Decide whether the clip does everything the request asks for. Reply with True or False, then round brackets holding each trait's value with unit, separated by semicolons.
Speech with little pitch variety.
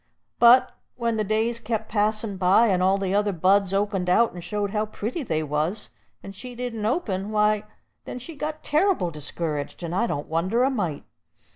False (4.1 semitones)